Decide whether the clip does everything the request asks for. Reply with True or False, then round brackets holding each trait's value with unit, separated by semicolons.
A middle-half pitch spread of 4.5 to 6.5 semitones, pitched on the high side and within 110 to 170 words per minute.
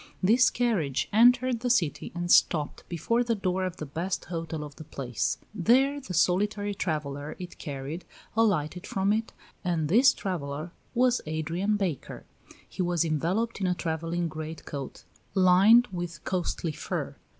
False (4.9 semitones; 180 Hz; 150 wpm)